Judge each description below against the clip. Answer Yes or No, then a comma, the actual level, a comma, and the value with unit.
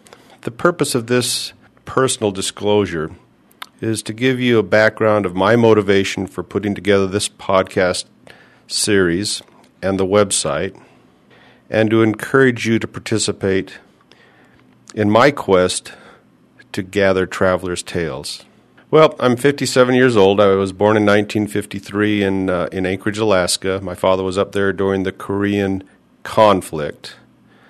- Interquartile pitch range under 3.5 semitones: Yes, average, 2.8 semitones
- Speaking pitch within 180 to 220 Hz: No, low, 105 Hz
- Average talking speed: No, slow, 130 wpm